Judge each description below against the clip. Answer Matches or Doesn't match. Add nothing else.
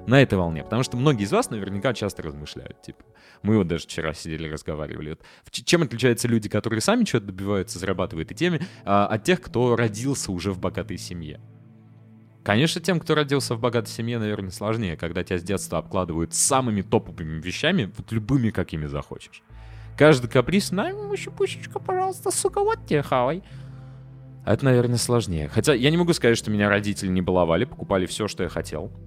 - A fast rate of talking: Matches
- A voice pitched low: Matches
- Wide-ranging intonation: Matches